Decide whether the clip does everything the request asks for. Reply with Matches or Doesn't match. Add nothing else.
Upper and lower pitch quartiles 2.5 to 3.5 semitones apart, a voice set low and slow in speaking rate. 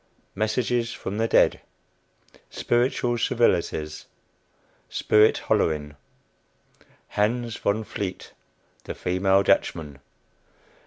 Doesn't match